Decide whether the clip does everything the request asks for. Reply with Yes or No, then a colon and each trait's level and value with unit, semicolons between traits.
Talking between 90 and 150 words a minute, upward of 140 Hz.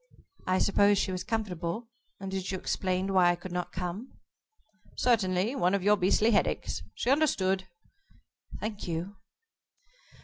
Yes: average, 145 wpm; high, 190 Hz